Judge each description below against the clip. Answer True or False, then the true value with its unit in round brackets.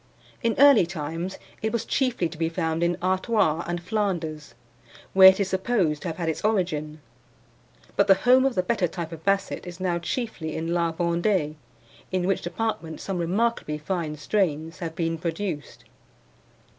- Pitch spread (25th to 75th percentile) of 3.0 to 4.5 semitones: True (3.4 semitones)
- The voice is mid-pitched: True (175 Hz)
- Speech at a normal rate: True (170 wpm)